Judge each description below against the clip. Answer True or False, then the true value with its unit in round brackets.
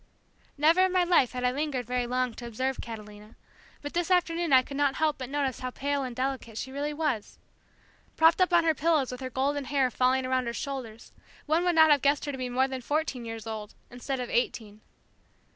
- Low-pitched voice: False (265 Hz)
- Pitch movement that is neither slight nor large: True (3.3 semitones)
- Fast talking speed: True (220 wpm)